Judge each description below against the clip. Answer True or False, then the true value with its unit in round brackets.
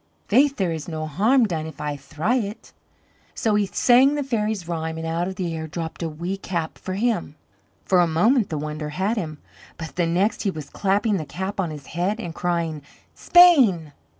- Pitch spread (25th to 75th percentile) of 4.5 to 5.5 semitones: True (4.8 semitones)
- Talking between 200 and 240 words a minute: True (205 wpm)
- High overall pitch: False (175 Hz)